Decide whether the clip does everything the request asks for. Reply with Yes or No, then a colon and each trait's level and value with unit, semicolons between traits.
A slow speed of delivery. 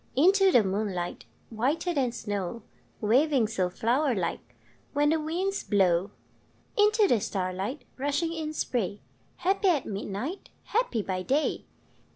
Yes: slow, 130 wpm